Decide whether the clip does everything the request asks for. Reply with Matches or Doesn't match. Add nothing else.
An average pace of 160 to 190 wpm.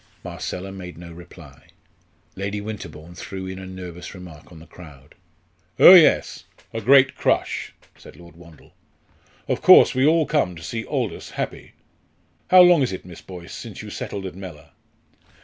Matches